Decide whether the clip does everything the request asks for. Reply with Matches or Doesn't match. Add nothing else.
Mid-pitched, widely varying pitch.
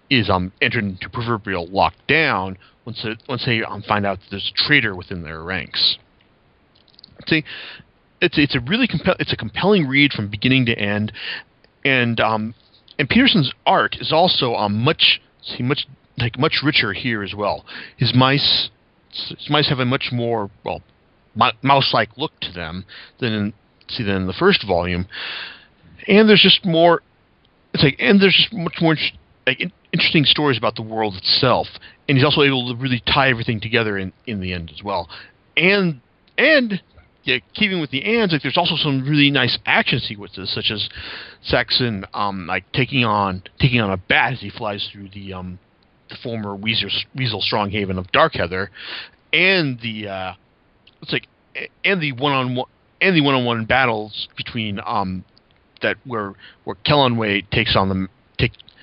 Doesn't match